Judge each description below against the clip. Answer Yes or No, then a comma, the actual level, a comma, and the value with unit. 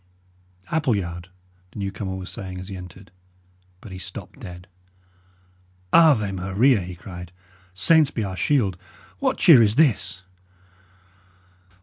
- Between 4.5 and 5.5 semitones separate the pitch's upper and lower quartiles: Yes, average, 5.2 semitones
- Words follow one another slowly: Yes, slow, 120 wpm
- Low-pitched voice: Yes, very low, 95 Hz